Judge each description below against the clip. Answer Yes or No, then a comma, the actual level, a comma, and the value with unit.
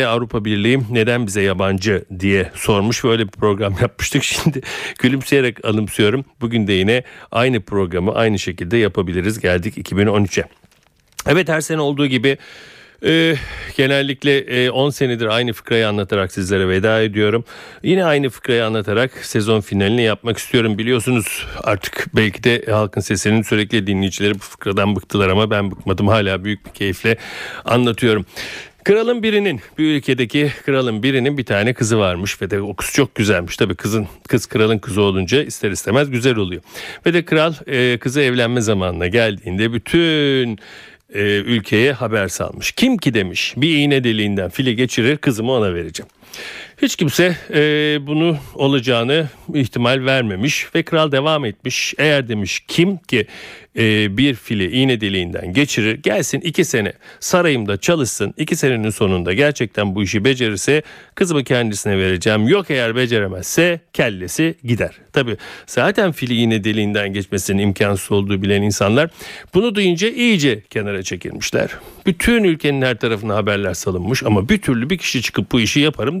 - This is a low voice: Yes, low, 115 Hz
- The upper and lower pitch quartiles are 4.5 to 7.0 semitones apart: Yes, average, 5.3 semitones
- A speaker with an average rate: No, fast, 150 wpm